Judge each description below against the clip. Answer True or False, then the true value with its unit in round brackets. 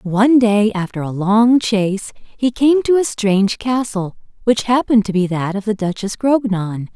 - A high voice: True (215 Hz)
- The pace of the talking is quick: False (180 wpm)